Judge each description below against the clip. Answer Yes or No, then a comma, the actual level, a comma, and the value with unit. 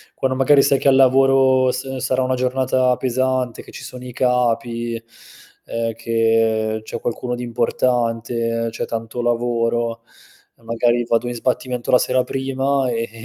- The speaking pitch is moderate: No, low, 120 Hz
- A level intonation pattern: Yes, narrow, 1.9 semitones